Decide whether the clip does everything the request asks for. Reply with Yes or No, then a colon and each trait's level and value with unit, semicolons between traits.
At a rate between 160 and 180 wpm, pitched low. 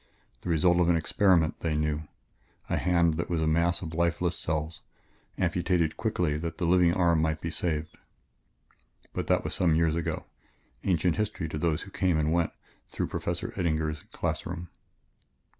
Yes: average, 175 wpm; very low, 85 Hz